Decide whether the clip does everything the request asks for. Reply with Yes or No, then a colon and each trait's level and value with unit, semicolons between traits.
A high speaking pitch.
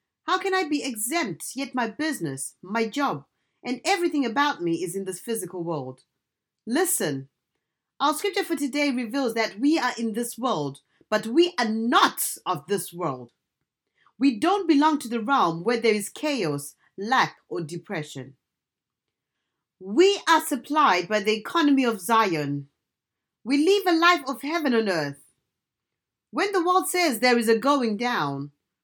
Yes: high, 235 Hz